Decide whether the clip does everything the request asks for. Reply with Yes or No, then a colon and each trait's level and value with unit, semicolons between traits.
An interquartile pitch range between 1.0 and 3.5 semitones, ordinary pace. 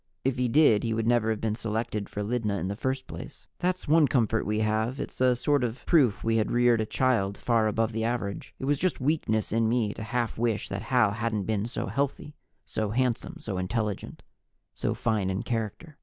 No: average, 2.8 semitones; fast, 215 wpm